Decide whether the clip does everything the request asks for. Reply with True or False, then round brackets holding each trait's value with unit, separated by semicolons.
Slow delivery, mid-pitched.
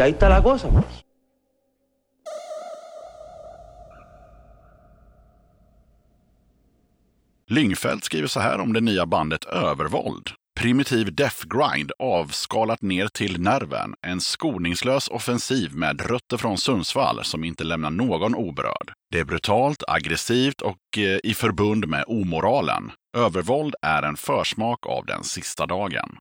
False (105 wpm; 120 Hz)